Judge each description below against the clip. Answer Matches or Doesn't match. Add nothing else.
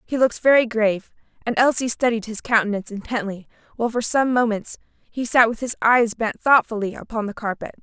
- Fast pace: Doesn't match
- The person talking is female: Matches